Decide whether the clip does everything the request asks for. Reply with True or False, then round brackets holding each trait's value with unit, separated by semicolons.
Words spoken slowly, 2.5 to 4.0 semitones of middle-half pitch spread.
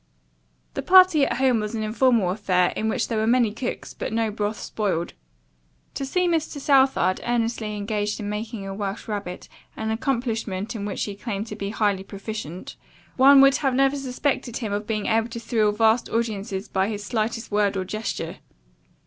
False (185 wpm; 2.9 semitones)